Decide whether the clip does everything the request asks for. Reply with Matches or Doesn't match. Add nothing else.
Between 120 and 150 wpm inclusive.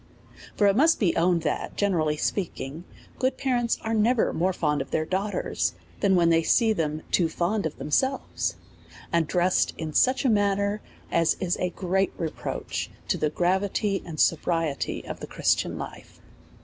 Doesn't match